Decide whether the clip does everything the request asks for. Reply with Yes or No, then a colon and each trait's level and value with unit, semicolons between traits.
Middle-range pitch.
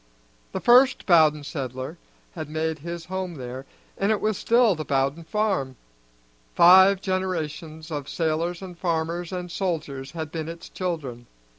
Yes: medium, 165 Hz